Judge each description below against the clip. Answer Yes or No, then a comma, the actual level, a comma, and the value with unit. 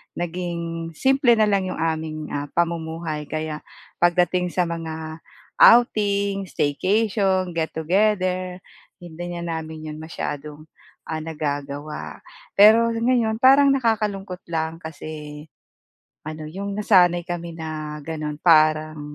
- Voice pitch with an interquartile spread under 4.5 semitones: Yes, average, 3.9 semitones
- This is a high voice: No, medium, 170 Hz